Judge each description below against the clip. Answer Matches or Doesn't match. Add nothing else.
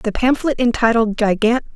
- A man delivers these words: Doesn't match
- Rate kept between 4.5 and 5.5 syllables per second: Matches